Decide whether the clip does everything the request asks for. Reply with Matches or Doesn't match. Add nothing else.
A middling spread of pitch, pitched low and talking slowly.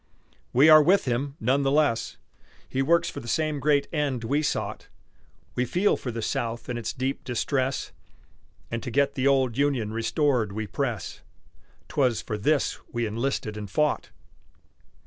Doesn't match